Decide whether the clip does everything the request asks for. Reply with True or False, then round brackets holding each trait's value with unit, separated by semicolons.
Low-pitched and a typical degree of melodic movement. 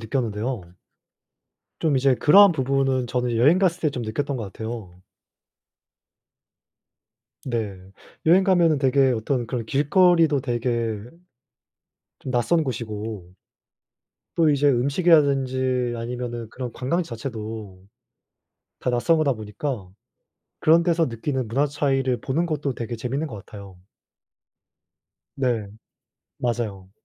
True (130 Hz; 4.0 semitones)